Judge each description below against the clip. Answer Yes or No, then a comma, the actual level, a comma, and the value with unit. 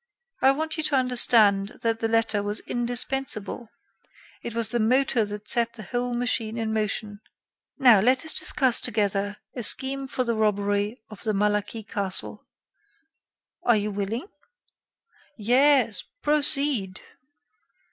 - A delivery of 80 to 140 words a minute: Yes, slow, 135 wpm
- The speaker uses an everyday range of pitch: Yes, average, 3.4 semitones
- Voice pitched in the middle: No, high, 225 Hz